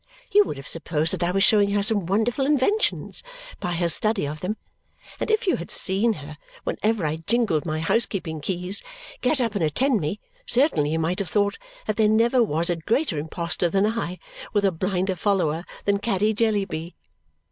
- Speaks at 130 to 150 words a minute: No, average, 190 wpm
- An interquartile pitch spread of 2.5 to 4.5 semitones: No, average, 5.0 semitones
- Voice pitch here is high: Yes, high, 195 Hz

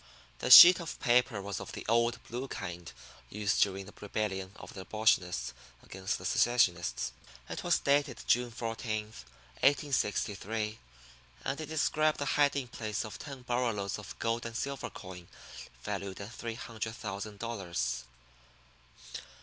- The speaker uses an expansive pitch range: No, average, 4.0 semitones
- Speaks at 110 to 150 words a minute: Yes, average, 145 wpm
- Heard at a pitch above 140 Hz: No, low, 110 Hz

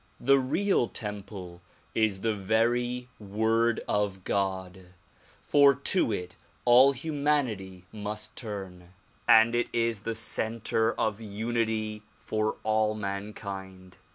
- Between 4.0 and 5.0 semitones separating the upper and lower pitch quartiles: No, average, 3.0 semitones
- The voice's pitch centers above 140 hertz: No, low, 110 Hz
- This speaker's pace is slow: Yes, slow, 110 wpm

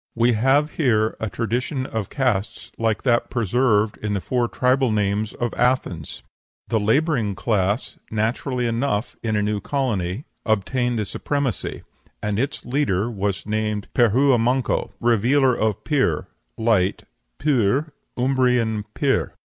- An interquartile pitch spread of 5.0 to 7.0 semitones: No, average, 3.6 semitones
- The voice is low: Yes, low, 115 Hz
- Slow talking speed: Yes, slow, 130 wpm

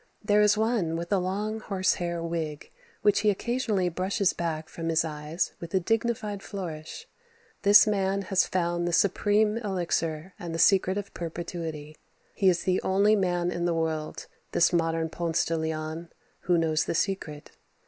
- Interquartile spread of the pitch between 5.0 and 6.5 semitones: No, average, 3.4 semitones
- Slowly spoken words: No, average, 170 wpm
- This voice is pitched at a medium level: Yes, medium, 175 Hz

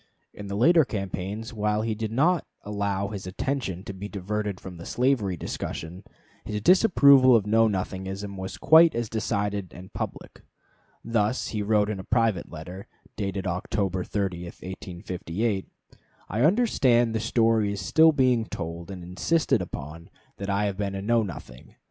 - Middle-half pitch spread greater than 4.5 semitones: No, average, 3.4 semitones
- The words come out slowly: No, average, 160 wpm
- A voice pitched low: Yes, low, 105 Hz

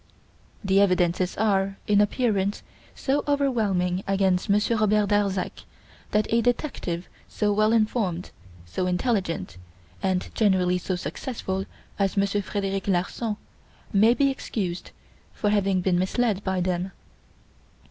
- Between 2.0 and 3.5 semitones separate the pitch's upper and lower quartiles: Yes, narrow, 2.5 semitones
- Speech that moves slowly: Yes, slow, 120 wpm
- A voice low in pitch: No, high, 195 Hz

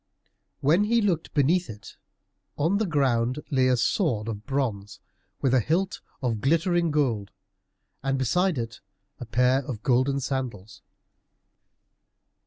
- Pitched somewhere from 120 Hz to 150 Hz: Yes, low, 135 Hz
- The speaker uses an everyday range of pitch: No, wide, 5.7 semitones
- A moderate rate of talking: No, slow, 130 wpm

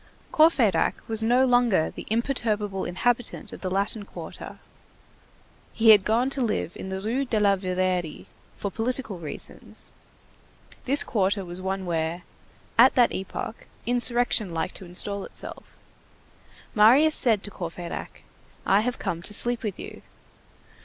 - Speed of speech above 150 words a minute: No, average, 140 wpm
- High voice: Yes, high, 210 Hz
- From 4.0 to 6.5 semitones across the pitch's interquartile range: Yes, average, 4.5 semitones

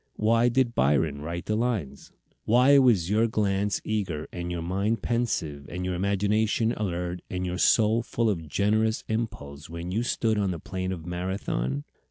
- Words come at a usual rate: Yes, average, 170 wpm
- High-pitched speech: No, low, 100 Hz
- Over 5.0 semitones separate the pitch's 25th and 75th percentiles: No, average, 4.3 semitones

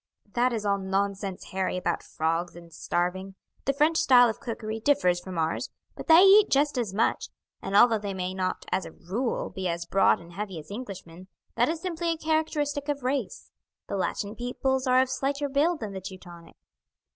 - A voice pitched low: No, high, 210 Hz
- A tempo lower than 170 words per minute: No, average, 190 wpm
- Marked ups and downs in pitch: Yes, wide, 6.9 semitones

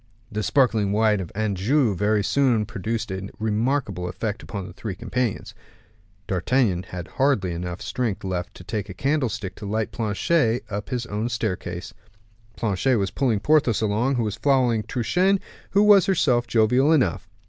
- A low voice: Yes, low, 110 Hz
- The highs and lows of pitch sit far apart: No, average, 4.2 semitones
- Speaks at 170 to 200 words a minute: No, average, 160 wpm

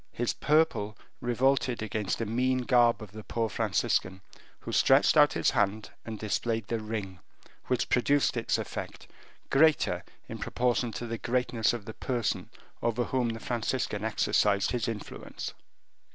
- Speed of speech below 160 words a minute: Yes, average, 150 wpm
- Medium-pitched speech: No, low, 115 Hz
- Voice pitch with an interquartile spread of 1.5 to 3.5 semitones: Yes, average, 2.7 semitones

